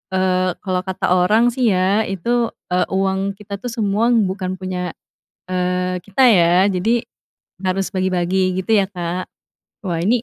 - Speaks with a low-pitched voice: No, high, 190 Hz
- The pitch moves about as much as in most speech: No, narrow, 2.2 semitones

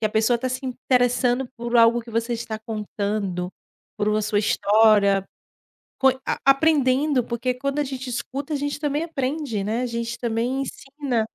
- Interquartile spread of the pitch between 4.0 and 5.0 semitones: No, average, 3.5 semitones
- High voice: Yes, high, 240 Hz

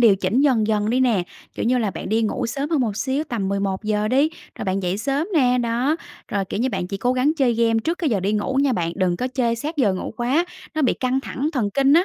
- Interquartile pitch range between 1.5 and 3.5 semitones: No, average, 4.7 semitones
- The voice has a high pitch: Yes, high, 235 Hz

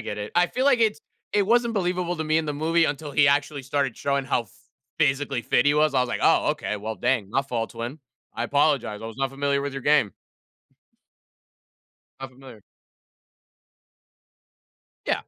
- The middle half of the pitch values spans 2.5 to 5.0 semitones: Yes, average, 3.9 semitones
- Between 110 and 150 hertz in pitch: Yes, medium, 140 Hz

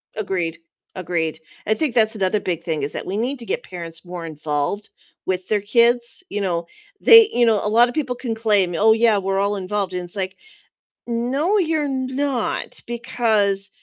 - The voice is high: Yes, high, 210 Hz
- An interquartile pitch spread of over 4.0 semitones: Yes, average, 4.7 semitones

